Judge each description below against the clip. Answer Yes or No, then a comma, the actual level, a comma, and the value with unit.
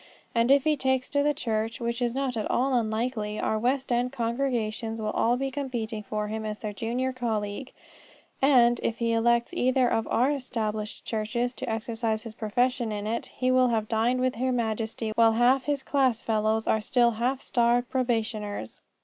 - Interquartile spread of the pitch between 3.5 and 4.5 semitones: No, average, 2.7 semitones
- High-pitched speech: Yes, high, 235 Hz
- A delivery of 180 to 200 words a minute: Yes, average, 190 wpm